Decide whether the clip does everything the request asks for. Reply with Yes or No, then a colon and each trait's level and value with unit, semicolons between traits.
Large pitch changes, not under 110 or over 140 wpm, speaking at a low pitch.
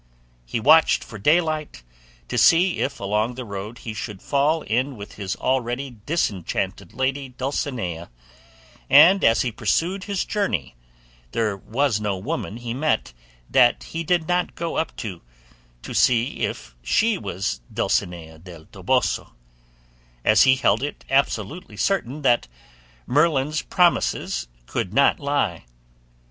Yes: wide, 6.8 semitones; slow, 135 wpm; low, 125 Hz